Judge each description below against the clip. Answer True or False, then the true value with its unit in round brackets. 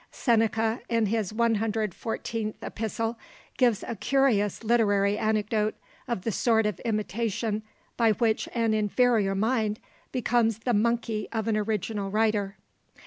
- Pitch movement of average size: False (1.6 semitones)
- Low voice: False (220 Hz)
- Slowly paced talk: True (125 wpm)